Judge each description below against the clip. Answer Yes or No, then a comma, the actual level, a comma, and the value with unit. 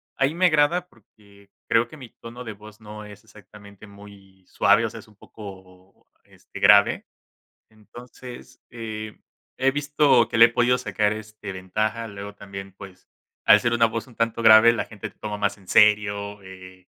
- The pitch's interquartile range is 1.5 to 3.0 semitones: Yes, narrow, 2.5 semitones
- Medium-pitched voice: No, low, 105 Hz